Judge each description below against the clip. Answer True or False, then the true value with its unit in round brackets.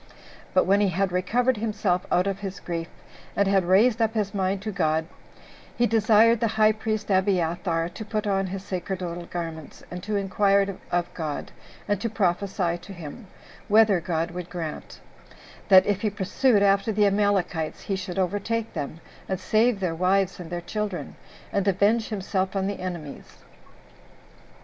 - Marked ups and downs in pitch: False (2.8 semitones)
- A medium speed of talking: True (165 wpm)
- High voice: True (195 Hz)